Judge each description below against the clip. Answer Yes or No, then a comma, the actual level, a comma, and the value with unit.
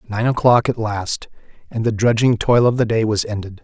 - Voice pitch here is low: Yes, low, 110 Hz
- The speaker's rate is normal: No, fast, 215 wpm